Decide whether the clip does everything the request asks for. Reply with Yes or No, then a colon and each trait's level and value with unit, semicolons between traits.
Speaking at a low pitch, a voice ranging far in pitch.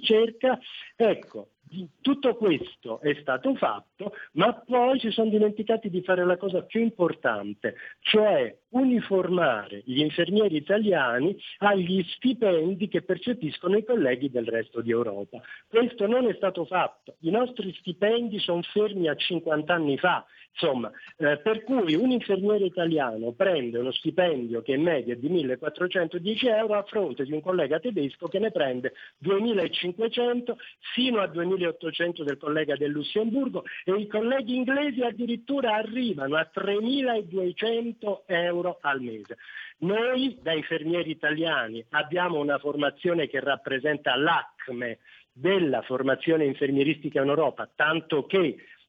No: medium, 180 Hz; wide, 6.8 semitones